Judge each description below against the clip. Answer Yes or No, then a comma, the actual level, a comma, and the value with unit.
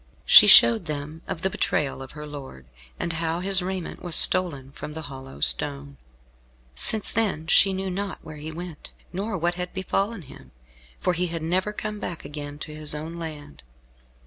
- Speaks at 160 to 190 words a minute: Yes, average, 175 wpm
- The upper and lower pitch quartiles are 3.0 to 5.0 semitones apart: Yes, average, 3.9 semitones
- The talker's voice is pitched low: No, medium, 160 Hz